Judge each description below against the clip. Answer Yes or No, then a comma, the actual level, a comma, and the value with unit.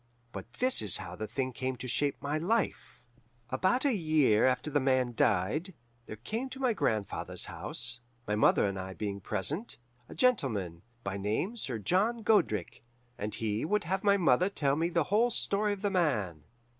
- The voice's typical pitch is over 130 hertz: Yes, medium, 140 Hz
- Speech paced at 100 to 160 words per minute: No, average, 180 wpm